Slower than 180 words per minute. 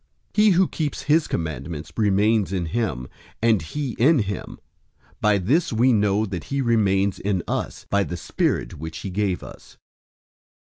Yes: average, 165 wpm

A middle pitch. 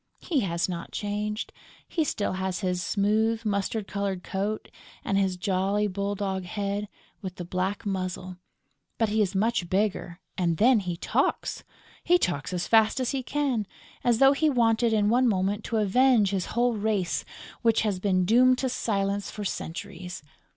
No: high, 205 Hz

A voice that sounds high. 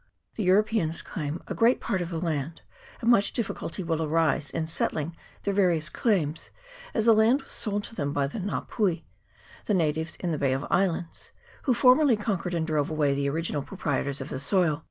No: medium, 170 Hz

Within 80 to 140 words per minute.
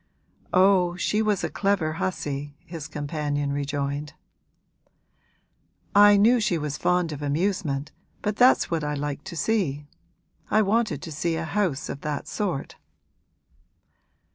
Yes: slow, 135 wpm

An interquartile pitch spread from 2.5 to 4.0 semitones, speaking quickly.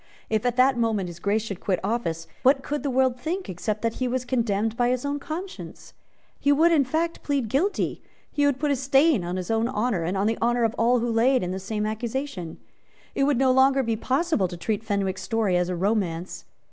No: average, 4.9 semitones; fast, 225 wpm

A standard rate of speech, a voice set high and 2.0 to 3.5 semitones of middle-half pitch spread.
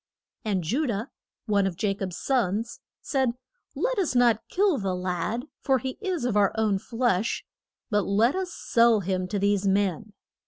No: average, 180 wpm; high, 215 Hz; average, 4.5 semitones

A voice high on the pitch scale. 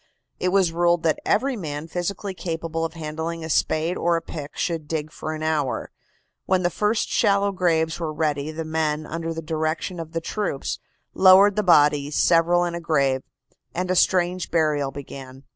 No: medium, 165 Hz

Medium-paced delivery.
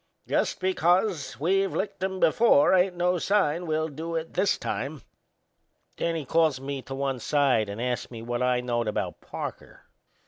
Yes: average, 170 wpm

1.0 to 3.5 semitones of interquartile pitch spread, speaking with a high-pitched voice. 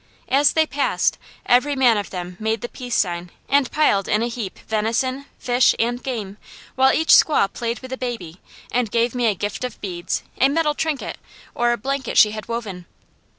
No: average, 4.0 semitones; high, 240 Hz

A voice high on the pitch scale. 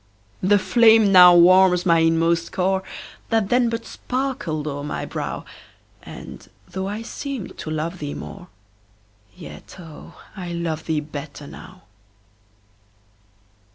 No: medium, 180 Hz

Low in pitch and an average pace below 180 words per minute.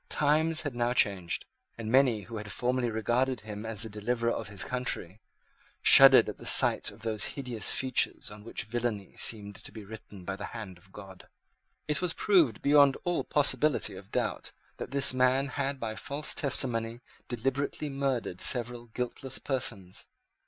Yes: low, 120 Hz; average, 165 wpm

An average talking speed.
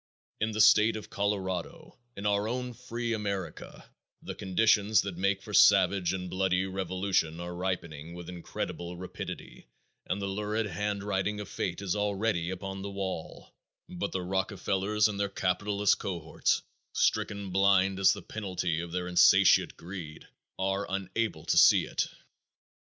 Yes: average, 145 wpm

